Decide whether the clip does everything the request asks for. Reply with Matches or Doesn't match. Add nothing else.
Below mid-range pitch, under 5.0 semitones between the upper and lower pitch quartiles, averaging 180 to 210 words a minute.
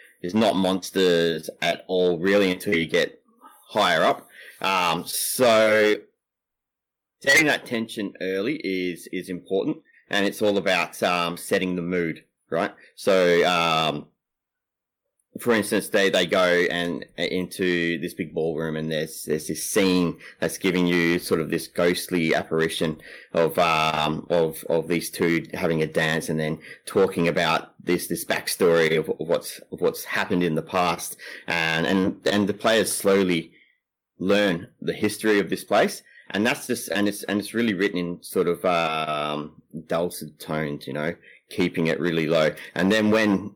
Doesn't match